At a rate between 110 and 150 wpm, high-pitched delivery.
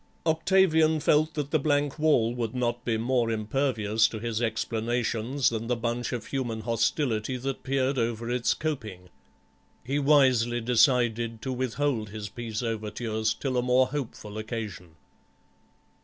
No: average, 140 wpm; low, 120 Hz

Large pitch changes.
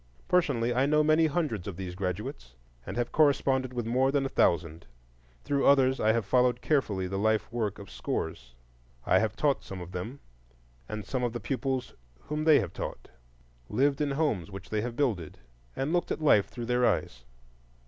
Yes: wide, 6.1 semitones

